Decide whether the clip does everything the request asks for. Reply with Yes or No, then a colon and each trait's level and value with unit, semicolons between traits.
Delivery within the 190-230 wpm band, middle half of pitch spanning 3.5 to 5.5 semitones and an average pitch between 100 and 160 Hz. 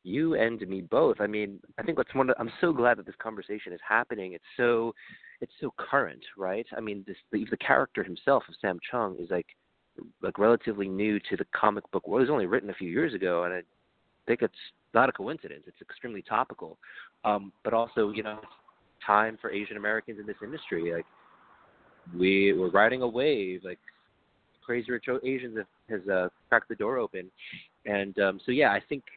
No: average, 200 wpm; narrow, 2.5 semitones; low, 105 Hz